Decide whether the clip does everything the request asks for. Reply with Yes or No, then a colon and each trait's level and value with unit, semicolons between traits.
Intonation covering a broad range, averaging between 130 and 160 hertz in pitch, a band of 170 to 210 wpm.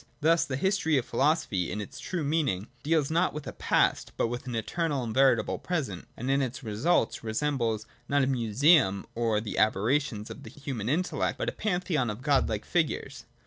Yes: wide, 5.7 semitones; low, 135 Hz; average, 185 wpm